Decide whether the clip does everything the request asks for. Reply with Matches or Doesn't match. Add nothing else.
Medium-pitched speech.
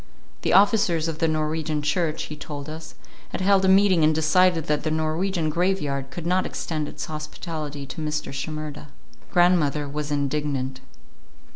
Matches